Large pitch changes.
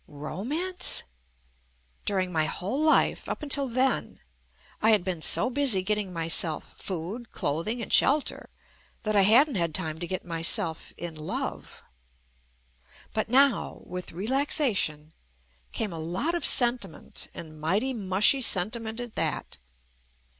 Yes: wide, 6.9 semitones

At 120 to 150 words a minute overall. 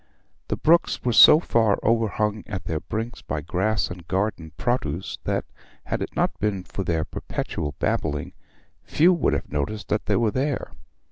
No: average, 165 wpm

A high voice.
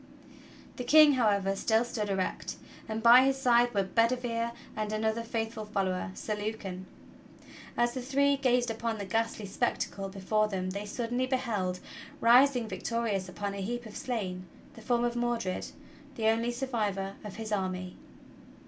Yes: high, 225 Hz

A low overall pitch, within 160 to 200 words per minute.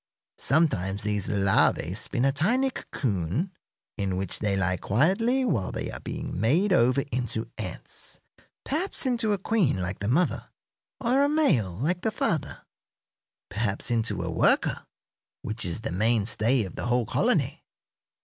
No: low, 120 Hz; average, 150 wpm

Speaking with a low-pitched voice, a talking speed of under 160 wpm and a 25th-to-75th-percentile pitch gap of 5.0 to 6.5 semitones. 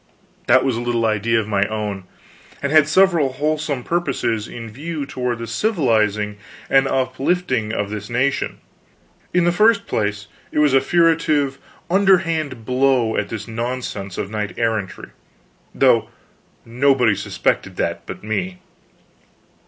Yes: low, 125 Hz; average, 140 wpm; wide, 5.5 semitones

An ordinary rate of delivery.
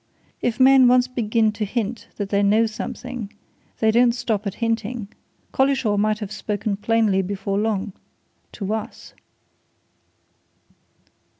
No: slow, 125 wpm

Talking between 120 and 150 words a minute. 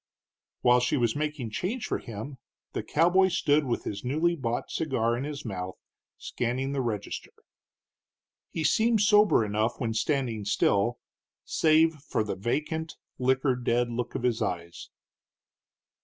Yes: average, 140 wpm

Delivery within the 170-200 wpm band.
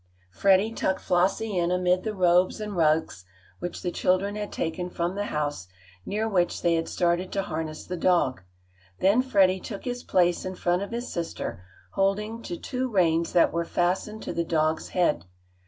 Yes: average, 180 wpm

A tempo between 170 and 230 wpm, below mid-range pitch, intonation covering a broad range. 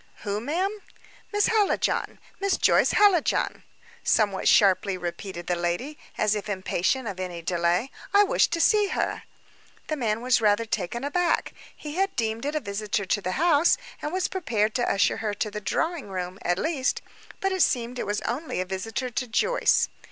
No: average, 180 wpm; high, 225 Hz; wide, 8.2 semitones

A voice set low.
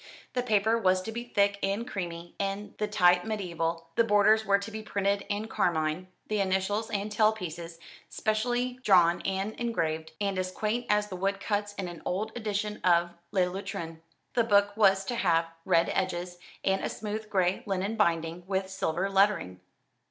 No: high, 195 Hz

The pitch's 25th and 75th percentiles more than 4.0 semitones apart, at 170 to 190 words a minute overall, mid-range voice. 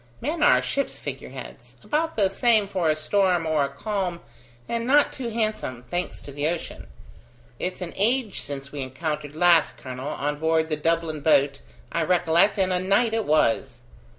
Yes: wide, 5.6 semitones; average, 180 wpm; medium, 170 Hz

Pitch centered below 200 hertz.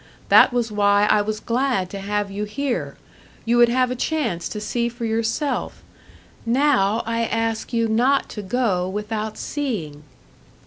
No: high, 225 Hz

